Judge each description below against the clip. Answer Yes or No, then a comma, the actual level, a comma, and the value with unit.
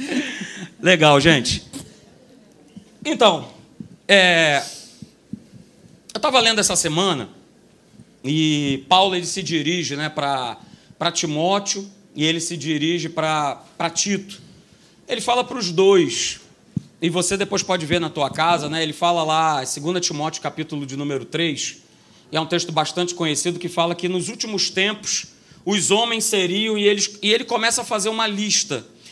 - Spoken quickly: No, average, 145 wpm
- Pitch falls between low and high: Yes, medium, 175 Hz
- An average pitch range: Yes, average, 4.2 semitones